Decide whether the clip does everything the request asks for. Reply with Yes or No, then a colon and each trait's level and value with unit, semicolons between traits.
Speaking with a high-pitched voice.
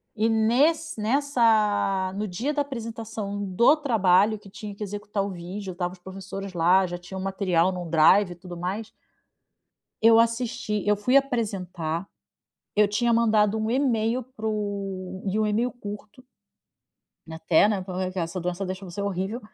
Yes: high, 205 Hz